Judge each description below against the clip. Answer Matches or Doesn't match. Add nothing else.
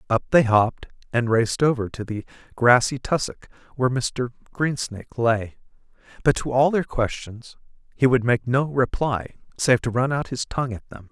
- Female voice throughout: Doesn't match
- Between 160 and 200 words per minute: Matches